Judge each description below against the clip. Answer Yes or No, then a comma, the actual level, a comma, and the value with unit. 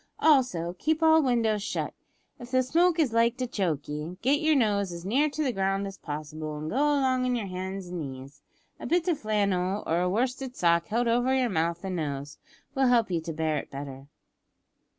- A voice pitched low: No, high, 205 Hz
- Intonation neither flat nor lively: No, wide, 7.3 semitones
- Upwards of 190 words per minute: Yes, fast, 205 wpm